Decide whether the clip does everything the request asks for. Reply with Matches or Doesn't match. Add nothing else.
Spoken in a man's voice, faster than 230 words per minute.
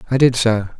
Doesn't match